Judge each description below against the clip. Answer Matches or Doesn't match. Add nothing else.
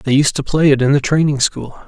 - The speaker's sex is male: Matches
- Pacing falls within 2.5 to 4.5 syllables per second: Doesn't match